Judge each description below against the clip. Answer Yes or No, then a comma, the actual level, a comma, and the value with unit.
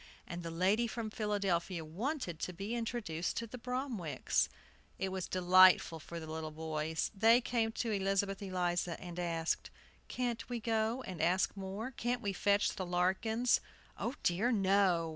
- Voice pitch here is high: Yes, high, 195 Hz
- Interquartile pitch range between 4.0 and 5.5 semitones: Yes, average, 4.6 semitones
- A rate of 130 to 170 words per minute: Yes, average, 160 wpm